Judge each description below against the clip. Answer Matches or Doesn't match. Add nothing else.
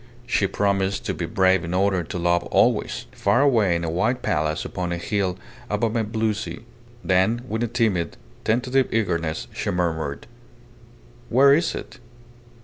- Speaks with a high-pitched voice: Doesn't match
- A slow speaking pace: Doesn't match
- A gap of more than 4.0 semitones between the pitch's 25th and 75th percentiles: Matches